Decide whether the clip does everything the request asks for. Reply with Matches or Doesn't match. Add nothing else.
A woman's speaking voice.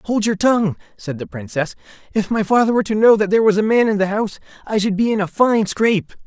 Doesn't match